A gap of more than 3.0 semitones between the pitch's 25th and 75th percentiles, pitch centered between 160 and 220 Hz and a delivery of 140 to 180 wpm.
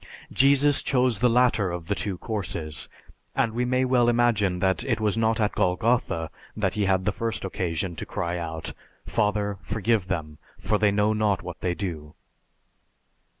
No: average, 4.4 semitones; low, 105 Hz; average, 170 wpm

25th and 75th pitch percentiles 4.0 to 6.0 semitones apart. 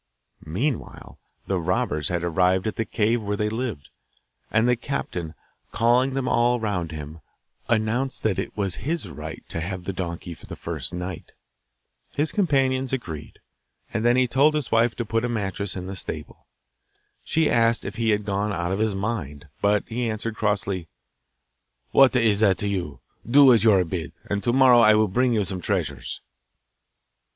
Yes: average, 4.7 semitones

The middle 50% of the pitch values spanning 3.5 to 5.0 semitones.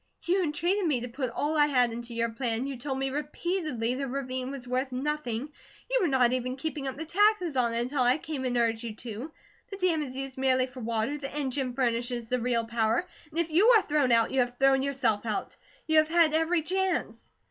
Yes: average, 3.9 semitones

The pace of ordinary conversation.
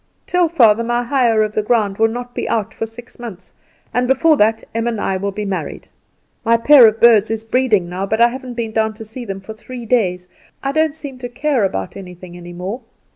No: fast, 230 wpm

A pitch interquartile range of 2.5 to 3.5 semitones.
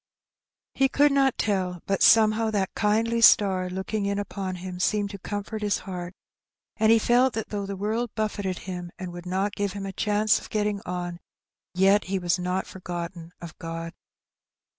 Yes: average, 2.9 semitones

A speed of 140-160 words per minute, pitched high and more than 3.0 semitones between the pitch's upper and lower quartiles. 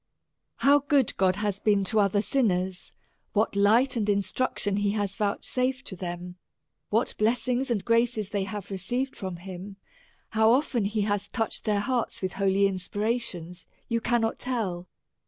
Yes: average, 155 wpm; high, 205 Hz; average, 3.5 semitones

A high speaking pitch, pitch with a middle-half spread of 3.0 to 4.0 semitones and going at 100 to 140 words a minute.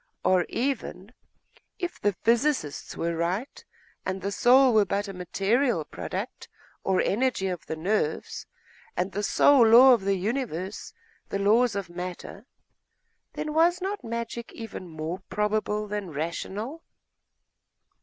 No: high, 205 Hz; average, 4.8 semitones; slow, 135 wpm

